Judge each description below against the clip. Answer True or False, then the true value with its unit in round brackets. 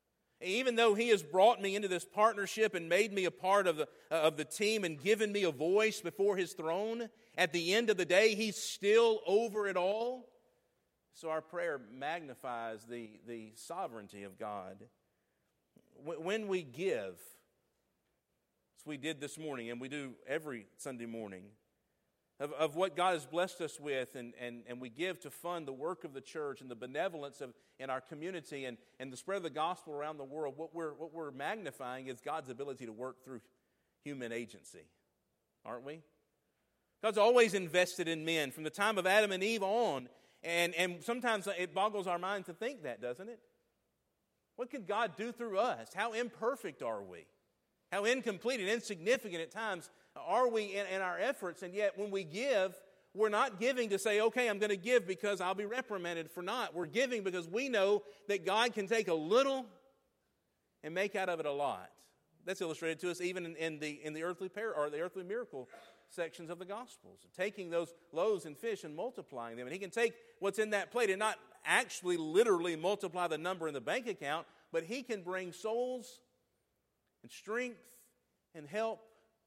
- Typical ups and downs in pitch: False (5.8 semitones)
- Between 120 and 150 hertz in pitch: False (185 Hz)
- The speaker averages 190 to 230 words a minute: True (195 wpm)